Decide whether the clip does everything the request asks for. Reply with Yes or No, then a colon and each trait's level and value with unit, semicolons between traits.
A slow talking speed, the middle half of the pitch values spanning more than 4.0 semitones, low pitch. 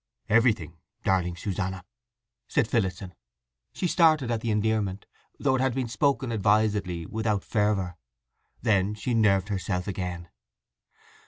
No: slow, 120 wpm; average, 3.7 semitones; low, 105 Hz